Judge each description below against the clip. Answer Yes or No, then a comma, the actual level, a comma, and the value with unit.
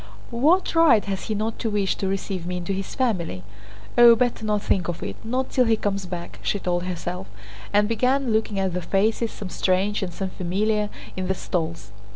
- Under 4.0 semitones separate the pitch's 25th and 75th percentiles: Yes, average, 3.5 semitones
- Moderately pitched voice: No, high, 200 Hz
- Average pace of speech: Yes, average, 195 wpm